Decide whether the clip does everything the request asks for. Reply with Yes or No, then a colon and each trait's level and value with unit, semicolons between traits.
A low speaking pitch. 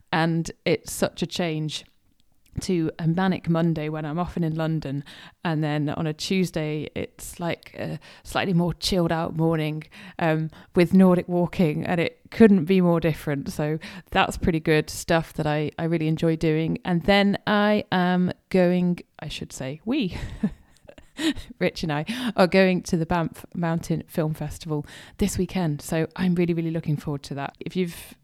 No: medium, 165 Hz